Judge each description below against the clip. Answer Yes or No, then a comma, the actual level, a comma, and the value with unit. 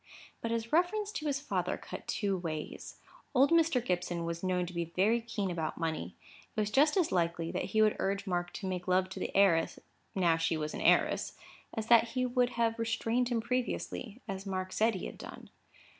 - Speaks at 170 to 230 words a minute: Yes, fast, 205 wpm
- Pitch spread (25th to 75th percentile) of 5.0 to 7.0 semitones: Yes, average, 5.3 semitones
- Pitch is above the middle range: Yes, high, 200 Hz